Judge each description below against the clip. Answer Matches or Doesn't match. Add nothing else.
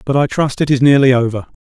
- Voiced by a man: Matches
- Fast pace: Matches